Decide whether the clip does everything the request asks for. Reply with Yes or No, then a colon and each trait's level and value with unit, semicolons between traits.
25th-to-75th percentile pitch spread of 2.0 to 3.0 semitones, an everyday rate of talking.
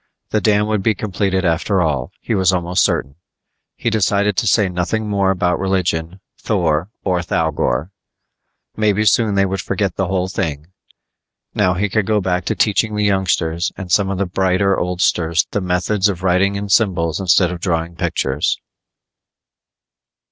Yes: narrow, 2.5 semitones; average, 160 wpm